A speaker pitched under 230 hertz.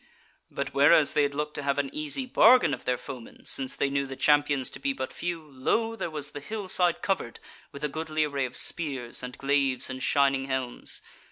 Yes: medium, 140 Hz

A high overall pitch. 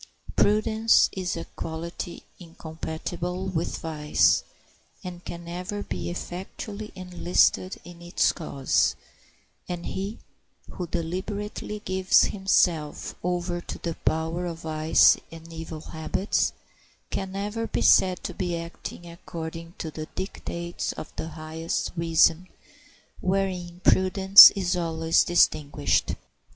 No: medium, 175 Hz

